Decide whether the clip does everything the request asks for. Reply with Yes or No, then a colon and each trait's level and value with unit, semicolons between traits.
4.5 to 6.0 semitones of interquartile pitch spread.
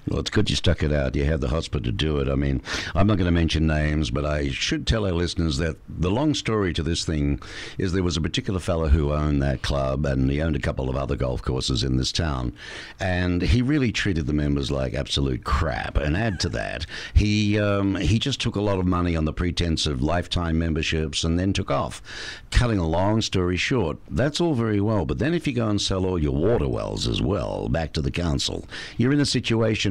Yes: wide, 5.5 semitones